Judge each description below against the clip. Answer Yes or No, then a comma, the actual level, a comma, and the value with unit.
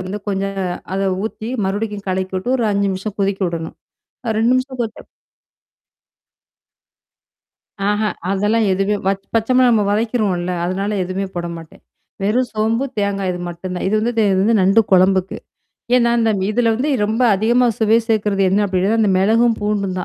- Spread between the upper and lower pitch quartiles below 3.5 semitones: Yes, average, 2.9 semitones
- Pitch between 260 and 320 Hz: No, high, 205 Hz